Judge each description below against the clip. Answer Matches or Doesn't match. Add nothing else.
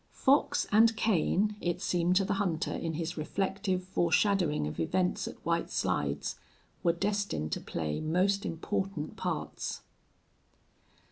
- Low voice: Doesn't match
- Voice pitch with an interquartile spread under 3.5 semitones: Doesn't match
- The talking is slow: Matches